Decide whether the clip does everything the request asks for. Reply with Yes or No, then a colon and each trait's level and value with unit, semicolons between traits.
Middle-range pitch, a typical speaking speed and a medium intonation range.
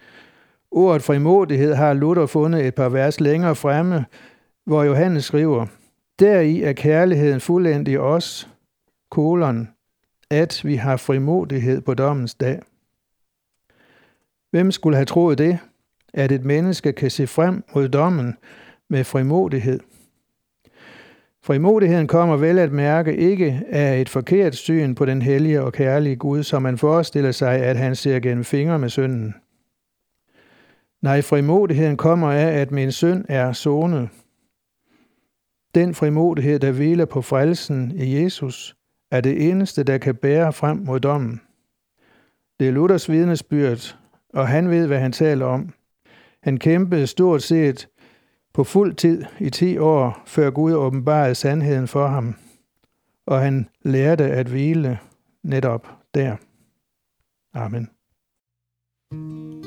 No: medium, 145 Hz; slow, 130 wpm; average, 3.5 semitones